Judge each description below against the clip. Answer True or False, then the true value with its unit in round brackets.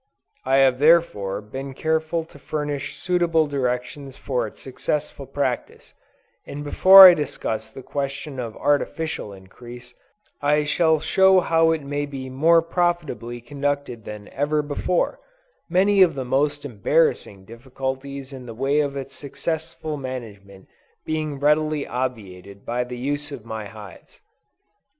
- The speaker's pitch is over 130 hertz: True (140 Hz)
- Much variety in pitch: False (3.9 semitones)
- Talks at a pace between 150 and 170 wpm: False (135 wpm)